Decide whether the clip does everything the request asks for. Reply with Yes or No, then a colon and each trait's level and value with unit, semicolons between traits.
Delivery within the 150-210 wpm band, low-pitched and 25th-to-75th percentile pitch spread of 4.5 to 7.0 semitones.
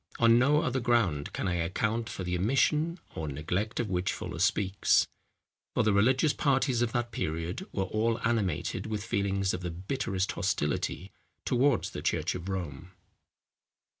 Yes: average, 160 wpm; low, 100 Hz; average, 4.9 semitones